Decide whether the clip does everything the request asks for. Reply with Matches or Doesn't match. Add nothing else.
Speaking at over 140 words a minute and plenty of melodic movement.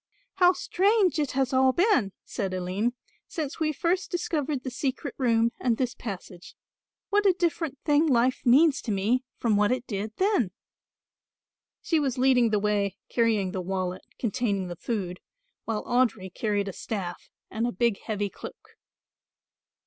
Matches